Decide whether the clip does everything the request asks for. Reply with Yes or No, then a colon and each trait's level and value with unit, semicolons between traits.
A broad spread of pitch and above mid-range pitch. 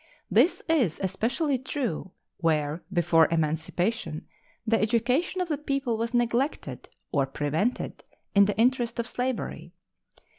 Yes: wide, 7.5 semitones; high, 225 Hz